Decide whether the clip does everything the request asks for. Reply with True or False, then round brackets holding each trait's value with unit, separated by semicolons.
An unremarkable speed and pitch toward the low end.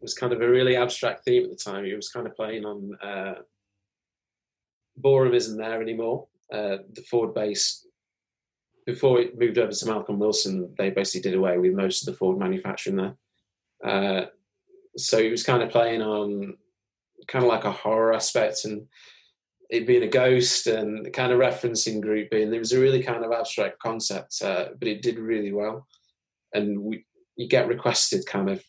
True (190 wpm; 115 Hz)